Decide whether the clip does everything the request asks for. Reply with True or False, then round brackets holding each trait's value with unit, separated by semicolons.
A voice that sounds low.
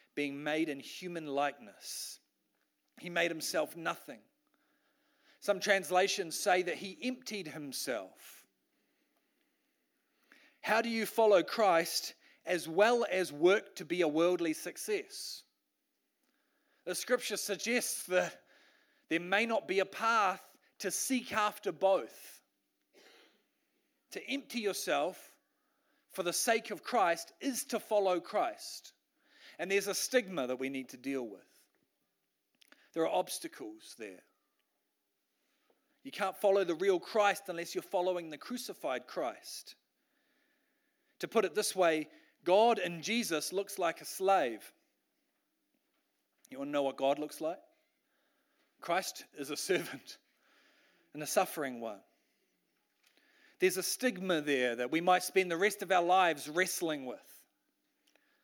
False (200 Hz)